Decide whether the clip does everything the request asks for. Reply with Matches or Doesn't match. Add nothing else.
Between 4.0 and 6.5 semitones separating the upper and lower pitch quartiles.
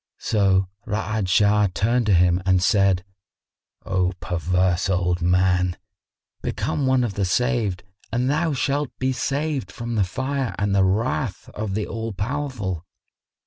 Matches